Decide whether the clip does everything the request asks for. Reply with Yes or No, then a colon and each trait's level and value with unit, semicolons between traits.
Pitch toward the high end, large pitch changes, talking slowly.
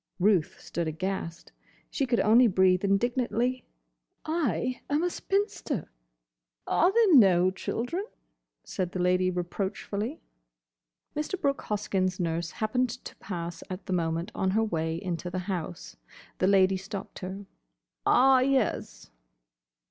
Yes: high, 195 Hz; wide, 5.7 semitones; slow, 125 wpm